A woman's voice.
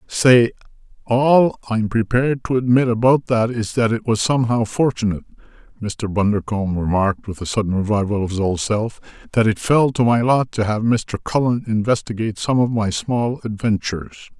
No: male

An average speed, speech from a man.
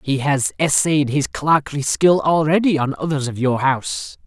Yes: average, 170 wpm; male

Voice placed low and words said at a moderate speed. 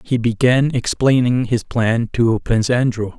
Yes: low, 120 Hz; average, 150 wpm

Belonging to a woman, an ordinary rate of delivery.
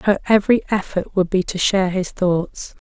Yes: female; average, 190 wpm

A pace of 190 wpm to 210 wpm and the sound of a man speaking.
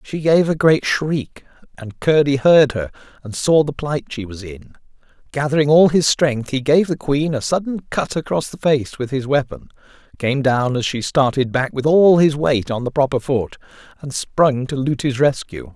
Yes: average, 200 wpm; male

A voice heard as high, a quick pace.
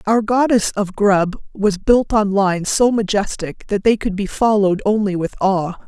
No: high, 205 Hz; average, 185 wpm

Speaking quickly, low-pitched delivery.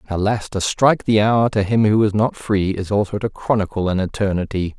Yes: fast, 215 wpm; low, 100 Hz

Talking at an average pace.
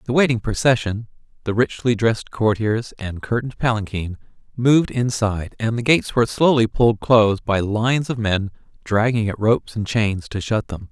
Yes: average, 170 wpm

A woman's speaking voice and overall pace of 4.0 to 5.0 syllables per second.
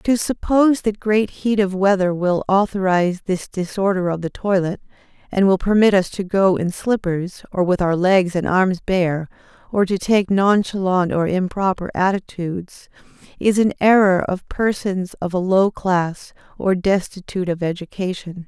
Yes: female; 4.6 syllables/s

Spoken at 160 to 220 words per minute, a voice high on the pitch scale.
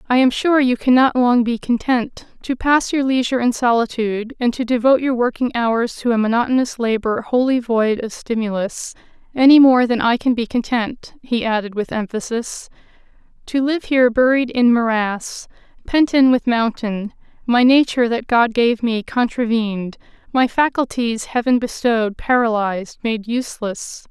No: average, 150 wpm; high, 240 Hz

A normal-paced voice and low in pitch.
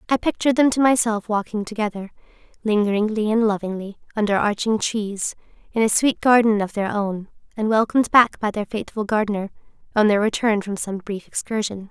No: average, 170 wpm; high, 210 Hz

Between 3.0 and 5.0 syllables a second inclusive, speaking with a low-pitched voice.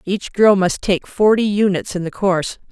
No: 4.8 syllables/s; high, 195 Hz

